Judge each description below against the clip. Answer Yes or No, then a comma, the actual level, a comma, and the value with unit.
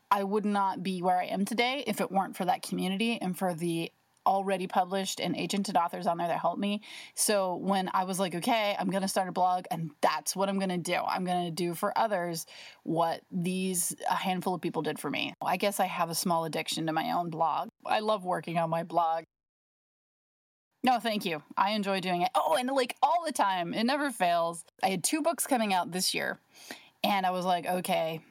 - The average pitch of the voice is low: No, medium, 185 Hz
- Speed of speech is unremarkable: No, fast, 220 wpm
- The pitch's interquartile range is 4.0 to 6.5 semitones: No, average, 2.9 semitones